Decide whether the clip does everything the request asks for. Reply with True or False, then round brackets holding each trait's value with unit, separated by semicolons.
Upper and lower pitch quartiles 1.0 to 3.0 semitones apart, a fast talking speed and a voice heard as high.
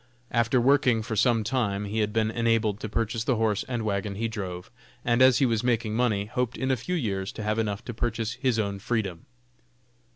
False (2.5 semitones; 215 wpm; 115 Hz)